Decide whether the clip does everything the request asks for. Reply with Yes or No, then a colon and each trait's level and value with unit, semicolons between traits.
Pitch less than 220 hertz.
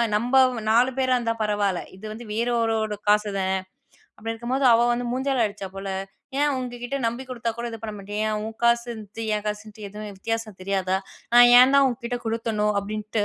No: high, 225 Hz